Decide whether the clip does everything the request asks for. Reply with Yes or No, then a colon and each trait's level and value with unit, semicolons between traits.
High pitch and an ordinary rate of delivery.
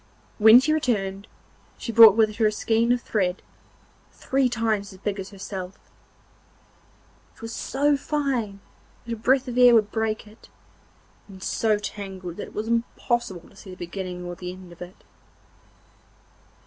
Yes: high, 215 Hz; average, 160 wpm